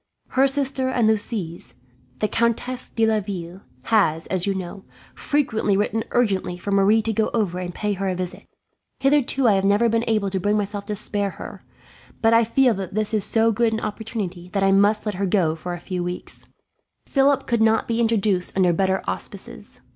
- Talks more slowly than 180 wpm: No, average, 195 wpm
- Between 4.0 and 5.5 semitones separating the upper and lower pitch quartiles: No, average, 3.0 semitones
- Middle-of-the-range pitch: No, high, 210 Hz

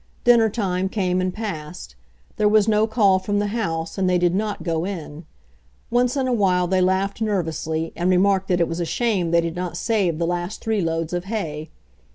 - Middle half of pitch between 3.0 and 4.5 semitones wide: Yes, average, 3.7 semitones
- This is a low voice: No, medium, 185 Hz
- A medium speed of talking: No, fast, 210 wpm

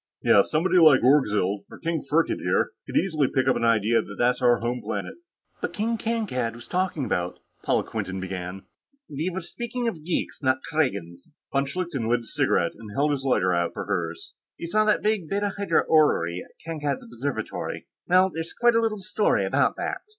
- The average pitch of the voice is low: No, medium, 145 Hz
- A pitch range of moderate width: No, wide, 8.0 semitones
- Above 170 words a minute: Yes, average, 190 wpm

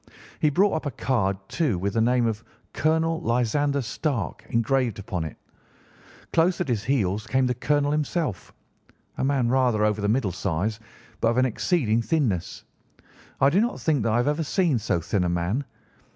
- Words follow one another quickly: No, average, 180 wpm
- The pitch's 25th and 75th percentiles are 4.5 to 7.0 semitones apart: Yes, wide, 5.4 semitones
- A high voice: No, low, 125 Hz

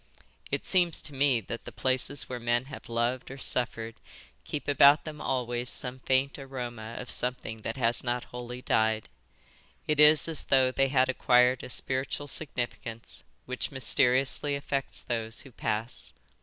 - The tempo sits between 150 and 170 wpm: Yes, average, 155 wpm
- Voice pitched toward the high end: No, low, 130 Hz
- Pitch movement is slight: Yes, narrow, 2.3 semitones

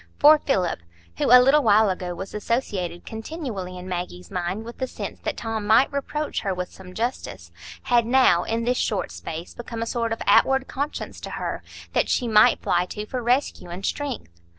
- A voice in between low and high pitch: No, high, 225 Hz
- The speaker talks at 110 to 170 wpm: No, average, 195 wpm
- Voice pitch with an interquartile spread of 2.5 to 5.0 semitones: No, wide, 5.6 semitones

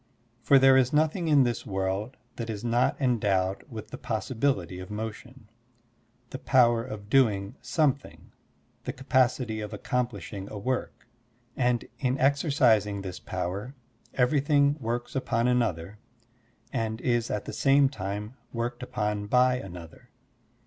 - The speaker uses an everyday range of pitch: Yes, average, 3.9 semitones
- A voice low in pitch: Yes, low, 120 Hz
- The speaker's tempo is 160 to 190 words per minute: No, slow, 135 wpm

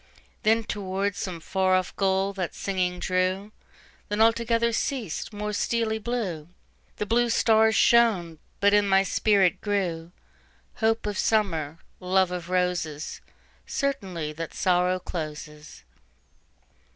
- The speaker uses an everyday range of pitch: Yes, average, 3.5 semitones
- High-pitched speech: Yes, high, 195 Hz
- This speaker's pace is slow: Yes, slow, 105 wpm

